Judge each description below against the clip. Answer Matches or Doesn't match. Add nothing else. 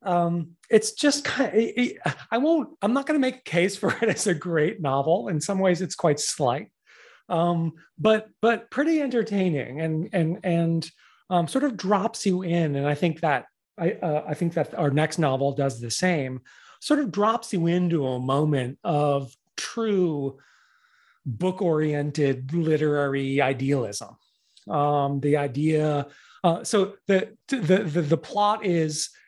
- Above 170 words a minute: Doesn't match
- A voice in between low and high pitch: Matches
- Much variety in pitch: Matches